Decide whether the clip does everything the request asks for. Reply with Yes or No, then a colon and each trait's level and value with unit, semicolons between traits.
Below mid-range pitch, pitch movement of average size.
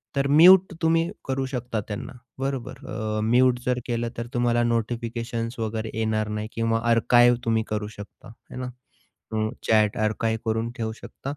No: low, 115 Hz; narrow, 2.1 semitones